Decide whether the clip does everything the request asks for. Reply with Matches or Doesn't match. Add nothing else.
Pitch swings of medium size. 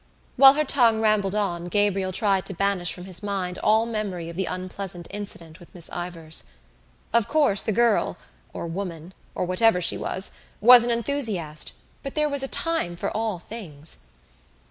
Matches